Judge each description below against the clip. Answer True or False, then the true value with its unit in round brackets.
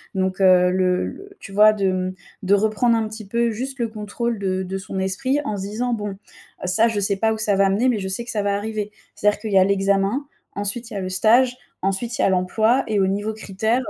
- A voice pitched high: True (205 Hz)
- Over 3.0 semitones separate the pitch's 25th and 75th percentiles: False (2.7 semitones)